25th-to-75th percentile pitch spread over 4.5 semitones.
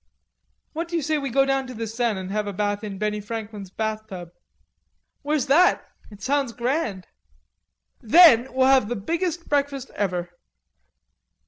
Yes: average, 5.2 semitones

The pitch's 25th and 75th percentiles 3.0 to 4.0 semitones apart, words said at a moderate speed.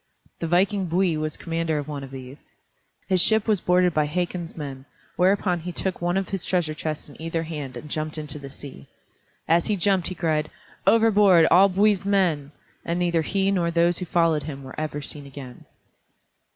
Yes: average, 3.4 semitones; average, 190 wpm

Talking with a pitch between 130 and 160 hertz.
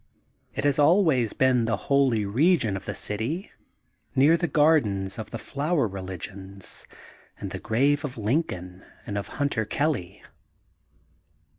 No: low, 120 Hz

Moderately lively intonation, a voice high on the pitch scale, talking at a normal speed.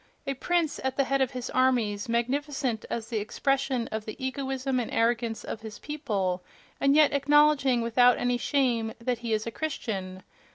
Yes: average, 3.5 semitones; very high, 250 Hz; average, 170 wpm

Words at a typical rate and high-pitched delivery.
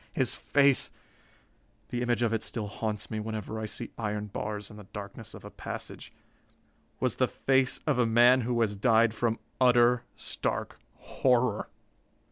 No: average, 160 wpm; low, 115 Hz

